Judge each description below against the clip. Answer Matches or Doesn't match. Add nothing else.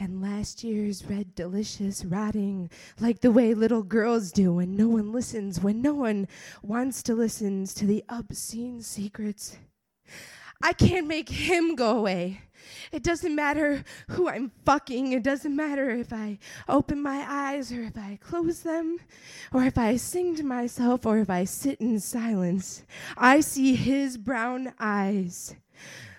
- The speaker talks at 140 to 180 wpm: Matches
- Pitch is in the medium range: Doesn't match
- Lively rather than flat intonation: Doesn't match